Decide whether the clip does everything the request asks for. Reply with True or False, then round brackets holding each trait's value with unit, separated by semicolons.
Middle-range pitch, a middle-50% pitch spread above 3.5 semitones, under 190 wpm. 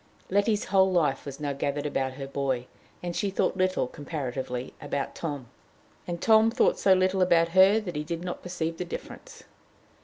True (165 Hz; 5.0 semitones; 180 wpm)